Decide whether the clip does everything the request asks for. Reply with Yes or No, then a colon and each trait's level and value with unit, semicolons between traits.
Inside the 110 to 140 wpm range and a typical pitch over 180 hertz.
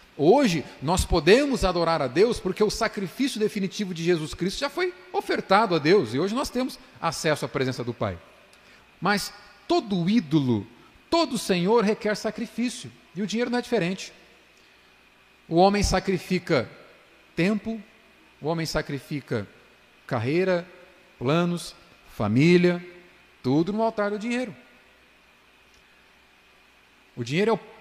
Yes: average, 125 wpm; high, 190 Hz